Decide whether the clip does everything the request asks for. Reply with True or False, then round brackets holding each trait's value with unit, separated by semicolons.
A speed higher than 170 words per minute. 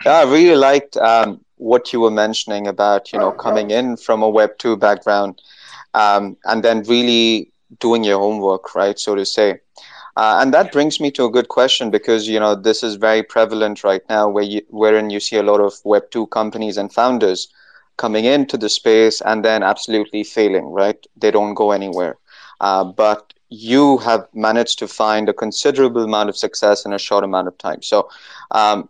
True (195 wpm)